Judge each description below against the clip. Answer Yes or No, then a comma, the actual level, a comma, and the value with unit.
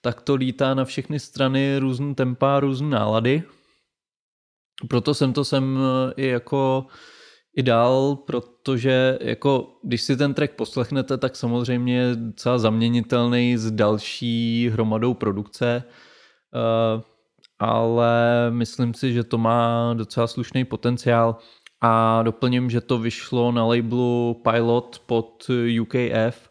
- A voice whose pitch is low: Yes, low, 120 Hz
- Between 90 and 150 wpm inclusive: Yes, average, 120 wpm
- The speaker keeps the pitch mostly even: Yes, narrow, 2.1 semitones